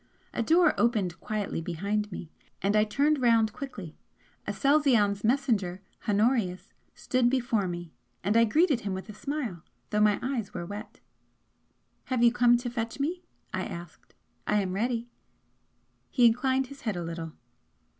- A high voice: Yes, high, 225 Hz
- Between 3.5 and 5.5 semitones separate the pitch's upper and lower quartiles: Yes, average, 4.4 semitones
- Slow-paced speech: No, average, 155 wpm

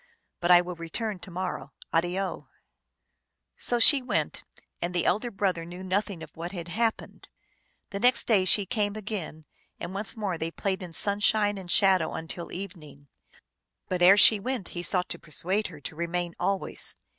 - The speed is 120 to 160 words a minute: No, average, 180 wpm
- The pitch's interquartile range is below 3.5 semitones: Yes, average, 3.0 semitones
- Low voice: No, medium, 185 Hz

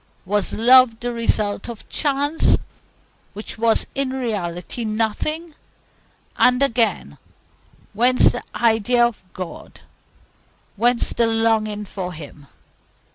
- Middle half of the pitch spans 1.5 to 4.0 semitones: Yes, average, 3.1 semitones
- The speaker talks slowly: Yes, slow, 105 wpm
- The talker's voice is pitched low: No, high, 225 Hz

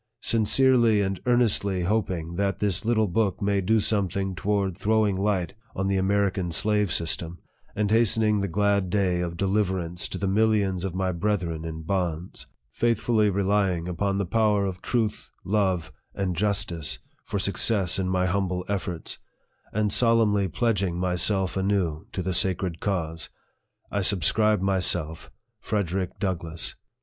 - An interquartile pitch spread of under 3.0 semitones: Yes, narrow, 2.6 semitones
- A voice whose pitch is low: Yes, very low, 95 Hz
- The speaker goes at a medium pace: Yes, average, 150 wpm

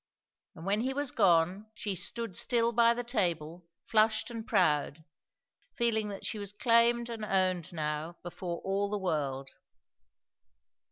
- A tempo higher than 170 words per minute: No, average, 145 wpm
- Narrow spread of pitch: No, average, 5.2 semitones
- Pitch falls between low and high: No, high, 200 Hz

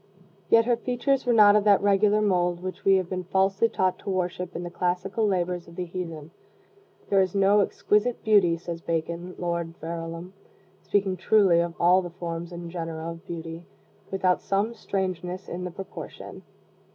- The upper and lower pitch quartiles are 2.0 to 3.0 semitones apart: Yes, narrow, 2.6 semitones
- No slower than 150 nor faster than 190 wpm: Yes, average, 175 wpm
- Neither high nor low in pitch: Yes, medium, 180 Hz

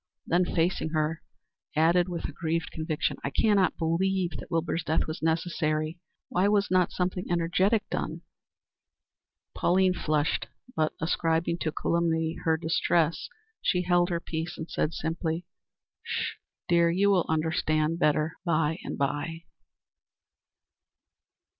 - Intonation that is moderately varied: No, narrow, 1.8 semitones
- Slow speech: Yes, slow, 125 wpm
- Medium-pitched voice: Yes, medium, 165 Hz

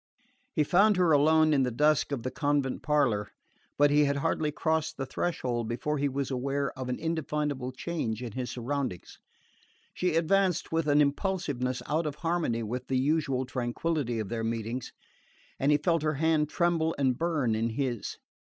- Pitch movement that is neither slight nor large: Yes, average, 3.9 semitones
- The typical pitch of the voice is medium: Yes, medium, 145 Hz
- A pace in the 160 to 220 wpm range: Yes, average, 175 wpm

